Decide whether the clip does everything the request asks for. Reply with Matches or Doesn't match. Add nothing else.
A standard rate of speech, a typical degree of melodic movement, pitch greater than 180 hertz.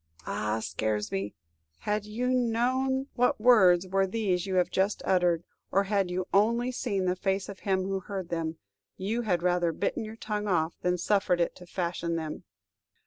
Matches